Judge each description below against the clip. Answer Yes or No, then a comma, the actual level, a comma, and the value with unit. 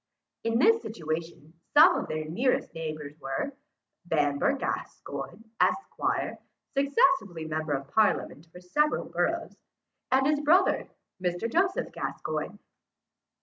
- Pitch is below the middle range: No, medium, 180 Hz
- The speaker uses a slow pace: Yes, slow, 110 wpm